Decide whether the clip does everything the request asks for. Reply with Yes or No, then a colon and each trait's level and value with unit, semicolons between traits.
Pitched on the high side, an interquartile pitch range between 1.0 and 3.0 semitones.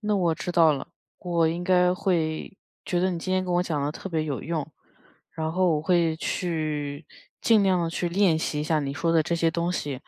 No: medium, 170 Hz; narrow, 2.4 semitones